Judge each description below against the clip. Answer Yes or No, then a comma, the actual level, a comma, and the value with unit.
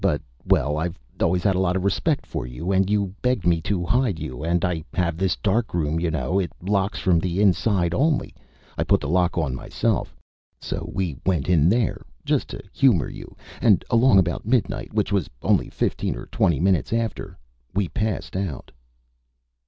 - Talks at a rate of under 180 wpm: No, average, 185 wpm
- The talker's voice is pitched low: Yes, very low, 95 Hz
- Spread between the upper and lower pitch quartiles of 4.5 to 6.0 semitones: No, average, 3.3 semitones